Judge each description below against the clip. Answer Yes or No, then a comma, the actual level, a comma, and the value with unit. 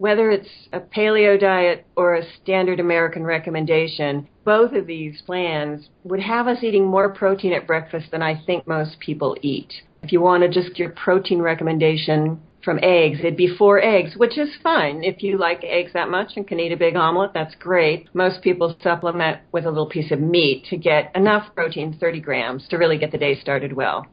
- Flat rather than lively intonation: No, average, 3.0 semitones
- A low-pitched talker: No, medium, 170 Hz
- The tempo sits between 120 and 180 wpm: No, average, 200 wpm